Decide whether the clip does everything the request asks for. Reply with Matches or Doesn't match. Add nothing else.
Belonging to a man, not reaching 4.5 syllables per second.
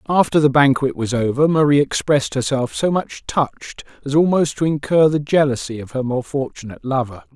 Doesn't match